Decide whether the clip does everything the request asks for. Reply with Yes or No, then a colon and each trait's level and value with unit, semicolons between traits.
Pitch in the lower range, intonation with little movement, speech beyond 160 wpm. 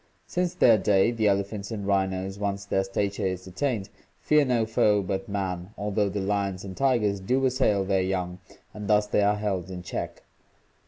Yes: low, 100 Hz; narrow, 1.9 semitones; average, 180 wpm